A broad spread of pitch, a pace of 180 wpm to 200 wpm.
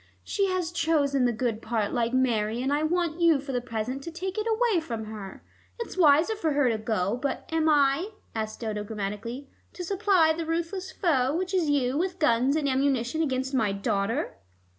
Yes: wide, 6.3 semitones; average, 195 wpm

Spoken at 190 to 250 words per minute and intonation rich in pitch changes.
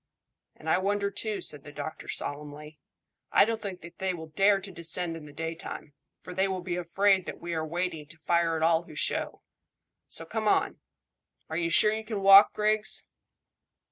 No: average, 195 wpm; average, 3.6 semitones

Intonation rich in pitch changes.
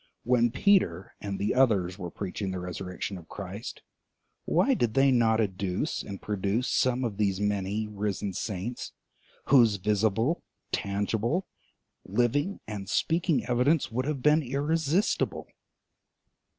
No: average, 4.7 semitones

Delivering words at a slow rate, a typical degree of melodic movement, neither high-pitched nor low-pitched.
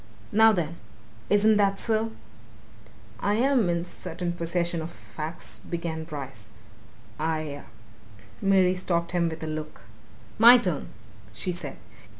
Yes: slow, 130 wpm; average, 4.0 semitones; medium, 170 Hz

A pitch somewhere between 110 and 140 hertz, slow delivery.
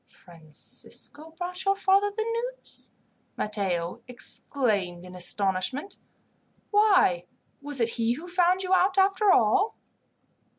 No: very high, 295 Hz; slow, 115 wpm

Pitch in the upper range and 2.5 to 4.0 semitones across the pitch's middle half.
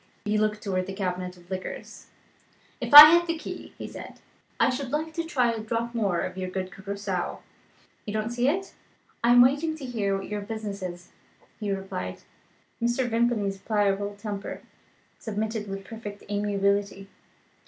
Yes: high, 210 Hz; average, 3.5 semitones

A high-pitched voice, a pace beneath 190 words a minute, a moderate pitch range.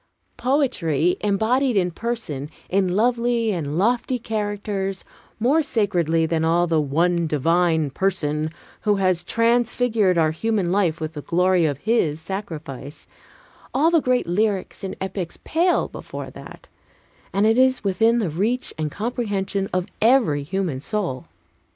No: high, 195 Hz; average, 140 wpm; wide, 5.7 semitones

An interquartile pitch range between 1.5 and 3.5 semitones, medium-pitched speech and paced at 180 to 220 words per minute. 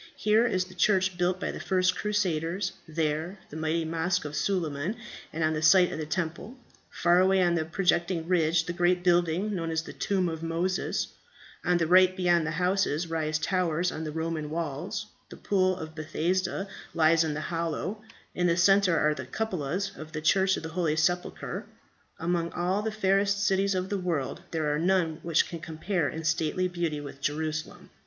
Yes: average, 2.8 semitones; medium, 170 Hz; average, 190 wpm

